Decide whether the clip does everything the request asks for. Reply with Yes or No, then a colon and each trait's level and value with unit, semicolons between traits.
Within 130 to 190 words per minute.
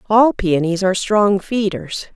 Yes: average, 140 wpm